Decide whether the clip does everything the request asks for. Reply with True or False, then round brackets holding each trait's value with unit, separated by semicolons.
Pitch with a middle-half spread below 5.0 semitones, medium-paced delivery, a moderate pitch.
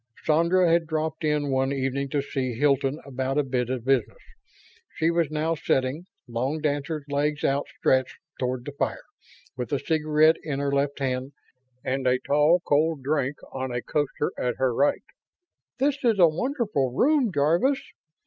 True (3.2 semitones; 165 wpm; 145 Hz)